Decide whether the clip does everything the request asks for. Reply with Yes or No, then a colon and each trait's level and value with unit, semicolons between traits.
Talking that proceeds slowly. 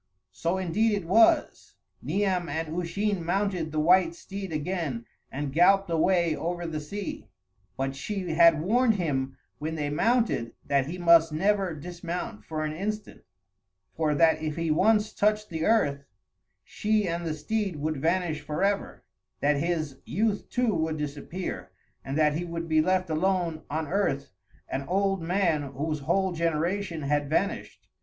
No: average, 155 wpm